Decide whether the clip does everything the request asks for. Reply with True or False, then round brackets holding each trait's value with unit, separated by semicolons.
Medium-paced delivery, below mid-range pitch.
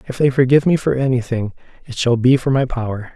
False (230 wpm; 125 Hz)